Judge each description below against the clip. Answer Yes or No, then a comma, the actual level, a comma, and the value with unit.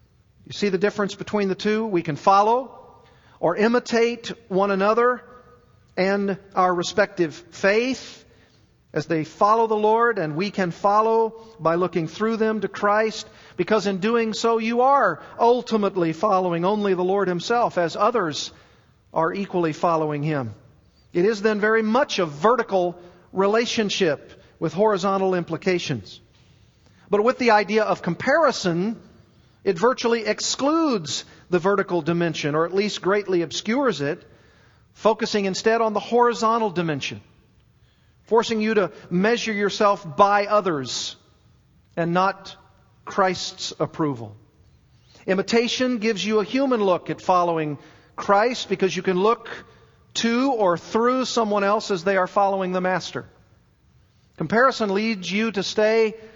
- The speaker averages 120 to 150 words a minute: Yes, slow, 135 wpm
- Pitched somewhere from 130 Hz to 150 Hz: No, high, 200 Hz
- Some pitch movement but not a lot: Yes, average, 4.3 semitones